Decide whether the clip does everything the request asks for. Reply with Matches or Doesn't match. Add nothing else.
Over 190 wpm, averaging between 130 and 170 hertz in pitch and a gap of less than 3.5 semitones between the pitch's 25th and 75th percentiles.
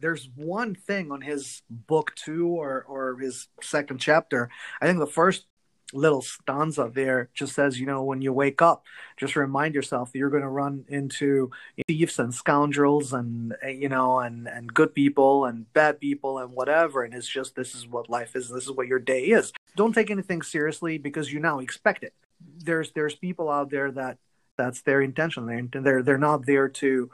Matches